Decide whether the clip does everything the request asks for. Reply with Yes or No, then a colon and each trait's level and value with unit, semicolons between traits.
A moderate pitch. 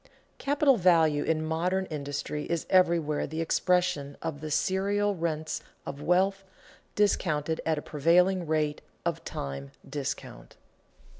Yes: medium, 160 Hz